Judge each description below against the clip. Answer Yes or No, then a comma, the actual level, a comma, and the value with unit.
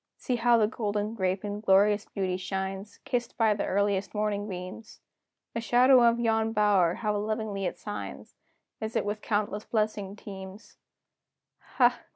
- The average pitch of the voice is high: Yes, high, 210 Hz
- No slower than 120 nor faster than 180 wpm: Yes, average, 155 wpm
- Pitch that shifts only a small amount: Yes, narrow, 2.1 semitones